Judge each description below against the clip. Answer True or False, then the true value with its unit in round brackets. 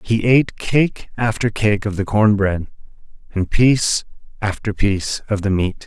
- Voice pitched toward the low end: True (105 Hz)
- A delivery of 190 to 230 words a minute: False (165 wpm)